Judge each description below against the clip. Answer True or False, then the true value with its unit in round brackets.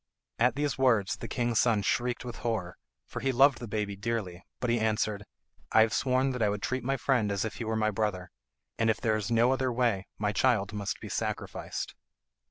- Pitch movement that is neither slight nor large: True (3.1 semitones)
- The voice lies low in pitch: True (115 Hz)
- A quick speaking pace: True (215 wpm)